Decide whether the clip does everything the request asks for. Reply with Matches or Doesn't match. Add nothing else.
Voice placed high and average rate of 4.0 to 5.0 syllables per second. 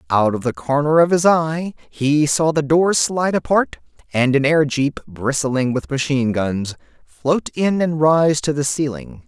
Doesn't match